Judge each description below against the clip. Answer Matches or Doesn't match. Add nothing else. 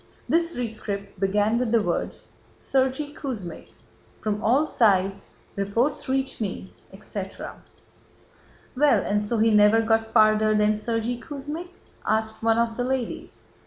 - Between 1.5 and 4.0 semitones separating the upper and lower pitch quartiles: Matches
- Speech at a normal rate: Doesn't match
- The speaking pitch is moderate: Doesn't match